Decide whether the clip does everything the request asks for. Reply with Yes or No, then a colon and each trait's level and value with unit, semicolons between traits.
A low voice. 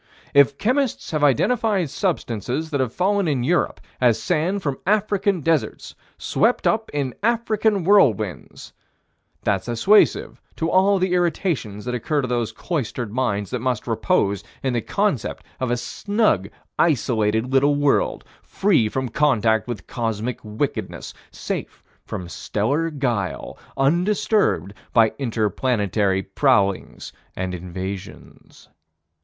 Yes: low, 130 Hz